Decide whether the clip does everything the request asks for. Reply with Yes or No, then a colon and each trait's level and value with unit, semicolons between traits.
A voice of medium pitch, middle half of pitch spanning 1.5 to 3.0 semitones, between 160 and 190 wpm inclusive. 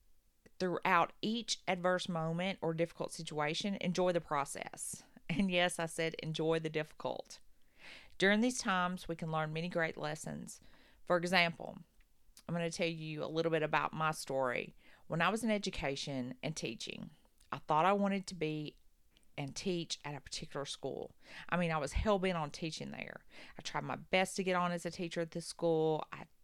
Yes: medium, 170 Hz; average, 2.7 semitones; average, 185 wpm